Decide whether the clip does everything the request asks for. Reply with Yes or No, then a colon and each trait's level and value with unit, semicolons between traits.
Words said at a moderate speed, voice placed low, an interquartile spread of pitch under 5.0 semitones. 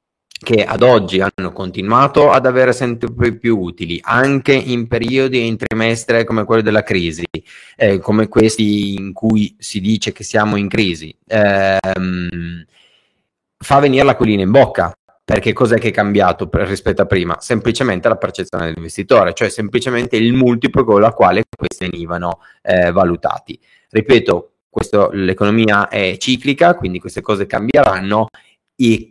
Yes: average, 150 wpm; low, 110 Hz; average, 3.8 semitones